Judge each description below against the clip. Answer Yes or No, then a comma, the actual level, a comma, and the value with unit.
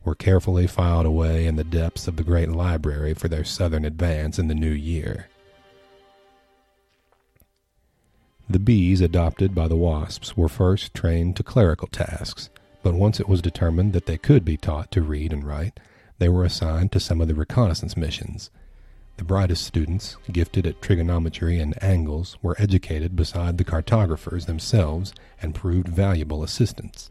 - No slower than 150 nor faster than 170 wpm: Yes, average, 160 wpm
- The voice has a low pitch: Yes, very low, 85 Hz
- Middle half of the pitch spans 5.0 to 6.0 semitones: No, average, 3.2 semitones